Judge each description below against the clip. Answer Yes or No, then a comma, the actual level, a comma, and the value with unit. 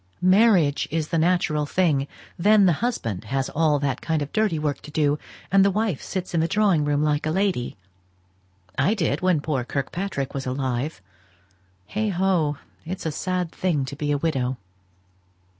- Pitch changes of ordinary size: Yes, average, 4.5 semitones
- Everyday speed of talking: Yes, average, 170 wpm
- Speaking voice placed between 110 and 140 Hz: No, medium, 155 Hz